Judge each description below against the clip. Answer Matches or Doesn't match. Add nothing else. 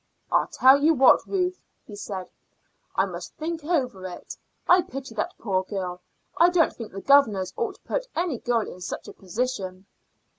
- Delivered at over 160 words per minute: Matches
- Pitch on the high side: Matches